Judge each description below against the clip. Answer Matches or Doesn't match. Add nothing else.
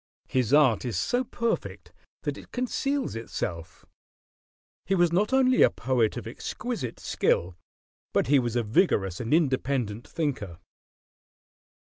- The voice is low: Matches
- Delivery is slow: Matches